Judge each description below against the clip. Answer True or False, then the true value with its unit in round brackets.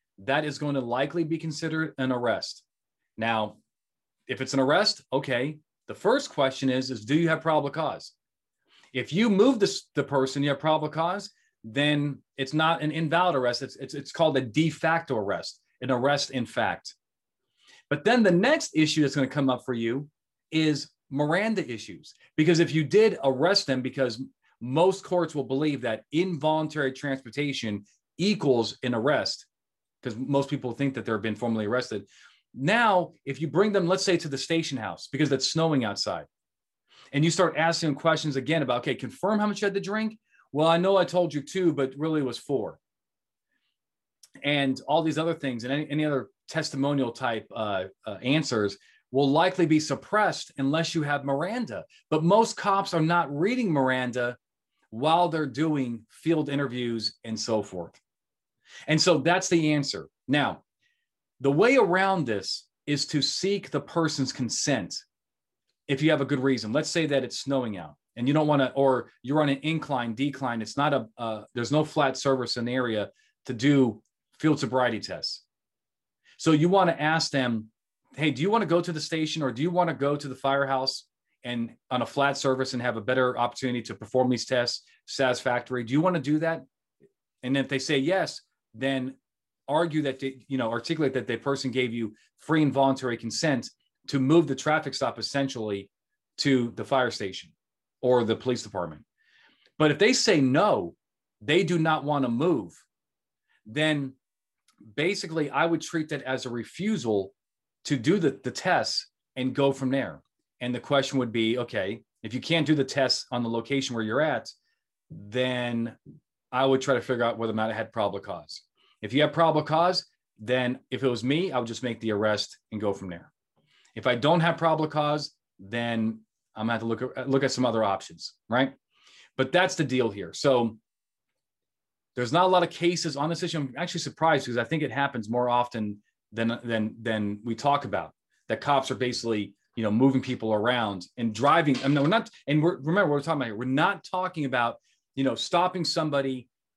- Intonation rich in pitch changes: False (4.4 semitones)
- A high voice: False (140 Hz)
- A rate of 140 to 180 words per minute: False (190 wpm)